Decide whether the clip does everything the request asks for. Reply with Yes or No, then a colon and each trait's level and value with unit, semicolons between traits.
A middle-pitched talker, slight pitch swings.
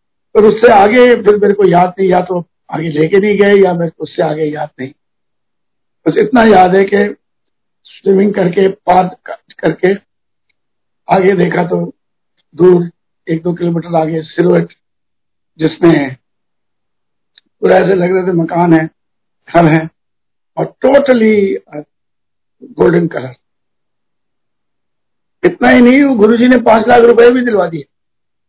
No: medium, 180 Hz; average, 4.3 semitones